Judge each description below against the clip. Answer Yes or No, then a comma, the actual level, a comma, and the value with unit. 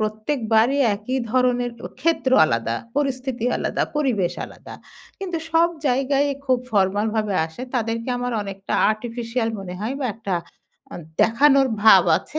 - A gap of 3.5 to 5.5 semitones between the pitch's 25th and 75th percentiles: Yes, average, 4.0 semitones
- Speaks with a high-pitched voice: Yes, high, 240 Hz